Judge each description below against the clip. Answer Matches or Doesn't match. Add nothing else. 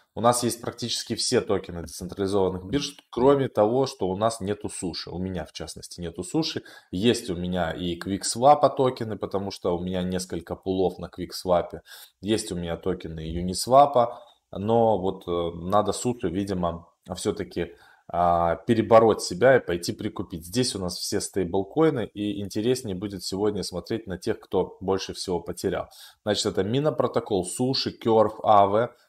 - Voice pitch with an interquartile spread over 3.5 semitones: Matches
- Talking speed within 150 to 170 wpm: Matches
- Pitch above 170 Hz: Doesn't match